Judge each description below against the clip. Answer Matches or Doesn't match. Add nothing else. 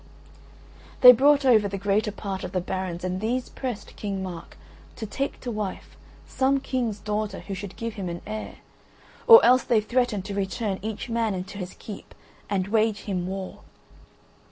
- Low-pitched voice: Doesn't match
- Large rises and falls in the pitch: Doesn't match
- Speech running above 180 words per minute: Doesn't match